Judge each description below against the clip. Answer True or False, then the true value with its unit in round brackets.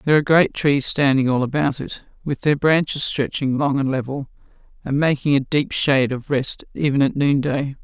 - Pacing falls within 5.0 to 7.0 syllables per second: True (5.3 syllables/s)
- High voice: False (140 Hz)